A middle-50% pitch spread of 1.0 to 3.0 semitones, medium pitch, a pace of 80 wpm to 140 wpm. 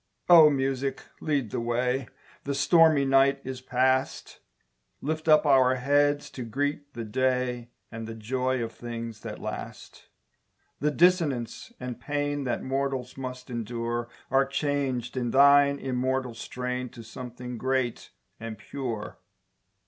No: narrow, 2.6 semitones; low, 130 Hz; slow, 135 wpm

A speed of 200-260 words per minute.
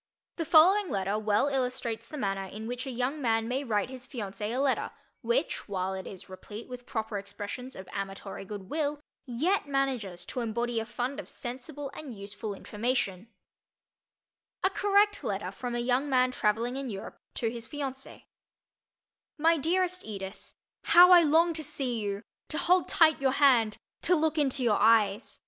No: average, 165 wpm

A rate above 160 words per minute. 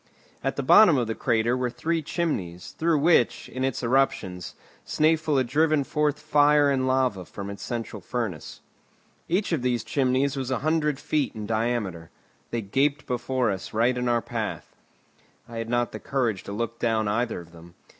Yes: average, 180 wpm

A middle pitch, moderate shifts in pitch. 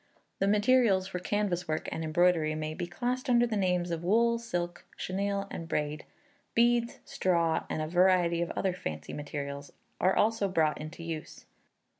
Yes: medium, 180 Hz; average, 4.3 semitones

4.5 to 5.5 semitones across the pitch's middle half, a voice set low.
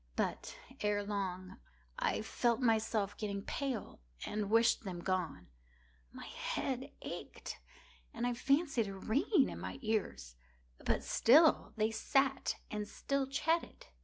No: average, 5.1 semitones; high, 220 Hz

